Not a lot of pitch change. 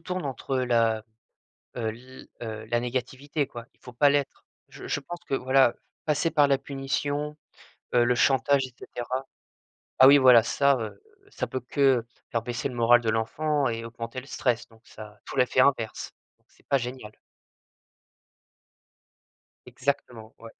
No: average, 3.1 semitones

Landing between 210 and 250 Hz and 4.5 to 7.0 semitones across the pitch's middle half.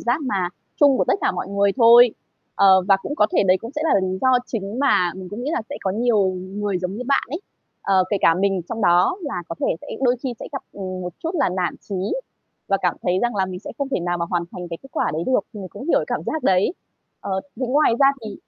No: high, 200 Hz; average, 5.2 semitones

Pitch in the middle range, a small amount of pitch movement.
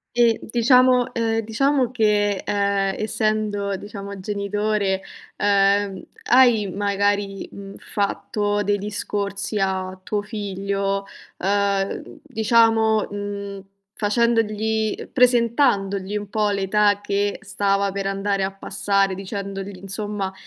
No: high, 205 Hz; narrow, 1.6 semitones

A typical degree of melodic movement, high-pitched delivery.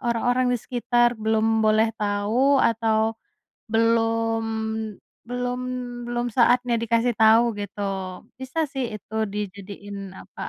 No: narrow, 2.0 semitones; high, 230 Hz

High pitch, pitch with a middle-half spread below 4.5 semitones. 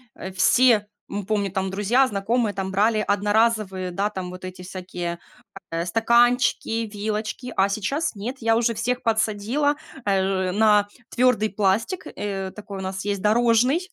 Yes: high, 210 Hz; average, 3.2 semitones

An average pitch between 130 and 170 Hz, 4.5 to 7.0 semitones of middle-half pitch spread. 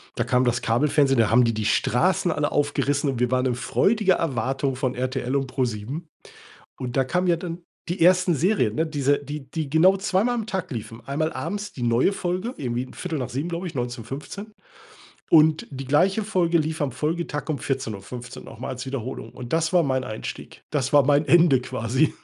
Yes: medium, 140 Hz; average, 5.2 semitones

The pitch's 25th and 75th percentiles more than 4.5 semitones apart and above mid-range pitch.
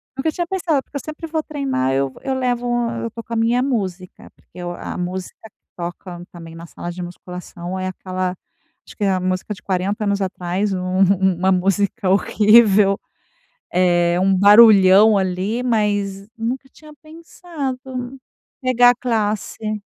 Yes: average, 4.9 semitones; high, 200 Hz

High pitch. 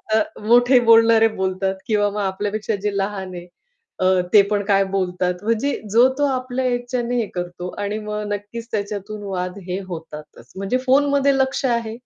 Yes: high, 210 Hz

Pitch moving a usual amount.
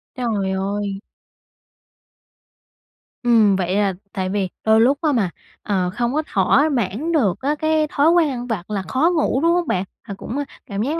No: wide, 6.7 semitones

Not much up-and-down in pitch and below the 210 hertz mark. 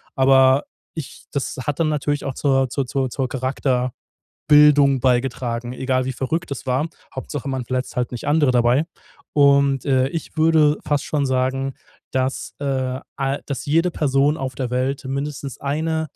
Yes: narrow, 2.0 semitones; low, 135 Hz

